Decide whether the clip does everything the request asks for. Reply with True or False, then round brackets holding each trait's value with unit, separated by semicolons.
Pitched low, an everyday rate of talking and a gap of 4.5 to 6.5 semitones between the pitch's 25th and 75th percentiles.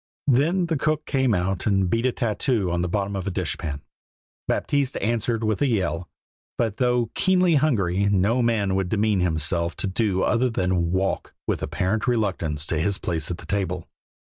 True (100 Hz; 180 wpm; 5.0 semitones)